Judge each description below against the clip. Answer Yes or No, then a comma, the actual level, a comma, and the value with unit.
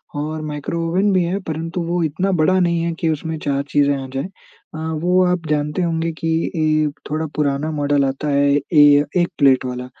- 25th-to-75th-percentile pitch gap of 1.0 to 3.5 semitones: Yes, average, 2.9 semitones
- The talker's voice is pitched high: No, medium, 155 Hz